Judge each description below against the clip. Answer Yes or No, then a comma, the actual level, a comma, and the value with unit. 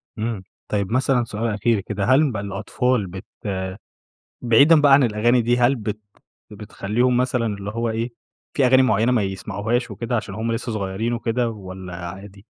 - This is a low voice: Yes, low, 115 Hz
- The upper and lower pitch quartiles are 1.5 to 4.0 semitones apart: Yes, average, 3.3 semitones